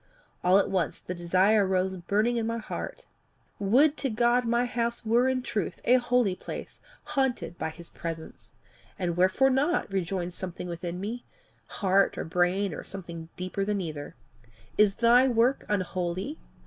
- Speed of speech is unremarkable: Yes, average, 160 wpm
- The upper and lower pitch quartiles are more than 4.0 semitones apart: Yes, average, 5.0 semitones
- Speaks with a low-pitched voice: No, high, 200 Hz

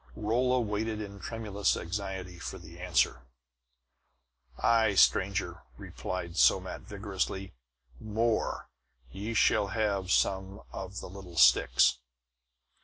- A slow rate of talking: Yes, slow, 105 wpm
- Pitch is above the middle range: No, low, 100 Hz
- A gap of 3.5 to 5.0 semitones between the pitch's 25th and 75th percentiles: No, narrow, 2.6 semitones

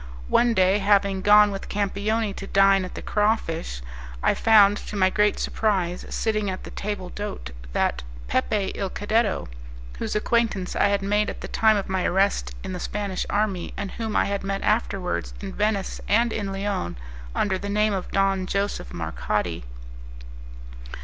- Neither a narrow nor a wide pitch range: No, narrow, 1.7 semitones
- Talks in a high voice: Yes, high, 200 Hz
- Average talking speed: Yes, average, 170 wpm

